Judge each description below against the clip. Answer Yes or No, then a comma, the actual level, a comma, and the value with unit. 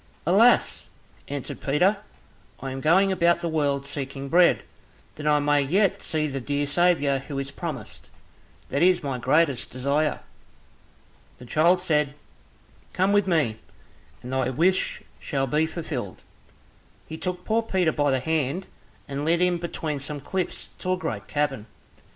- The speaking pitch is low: No, medium, 150 Hz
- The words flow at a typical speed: Yes, average, 150 wpm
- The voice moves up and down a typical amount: Yes, average, 4.1 semitones